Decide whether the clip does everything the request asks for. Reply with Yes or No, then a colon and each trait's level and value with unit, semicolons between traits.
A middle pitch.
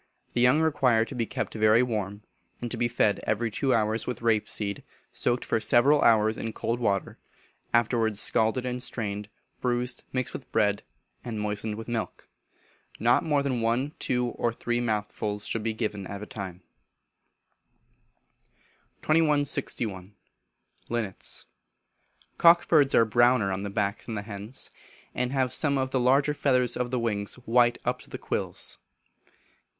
No: low, 115 Hz